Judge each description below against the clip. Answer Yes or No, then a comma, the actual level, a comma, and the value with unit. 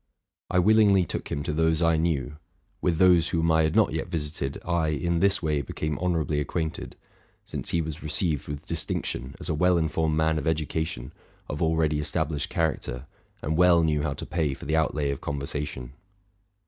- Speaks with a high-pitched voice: No, very low, 80 Hz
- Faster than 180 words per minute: Yes, average, 190 wpm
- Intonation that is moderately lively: No, narrow, 2.2 semitones